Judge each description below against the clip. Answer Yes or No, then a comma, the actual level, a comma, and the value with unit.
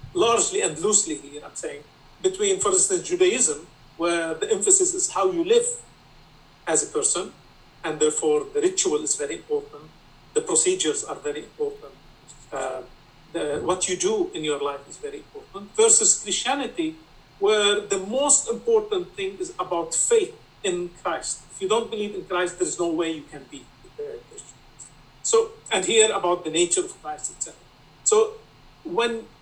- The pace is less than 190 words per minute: Yes, average, 165 wpm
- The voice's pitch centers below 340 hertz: No, very high, 370 Hz